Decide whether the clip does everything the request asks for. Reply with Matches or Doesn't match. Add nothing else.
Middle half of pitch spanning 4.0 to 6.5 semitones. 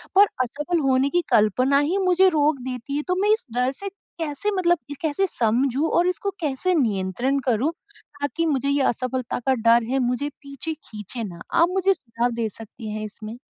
Matches